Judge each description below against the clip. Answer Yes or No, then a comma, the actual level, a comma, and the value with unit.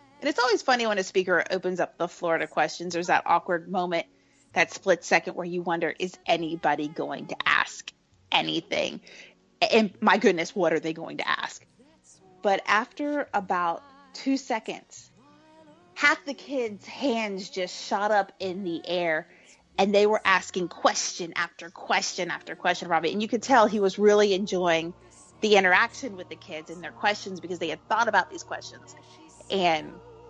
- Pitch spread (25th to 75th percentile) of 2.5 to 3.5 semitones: No, average, 4.5 semitones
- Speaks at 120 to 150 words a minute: No, average, 170 wpm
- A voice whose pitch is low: No, high, 190 Hz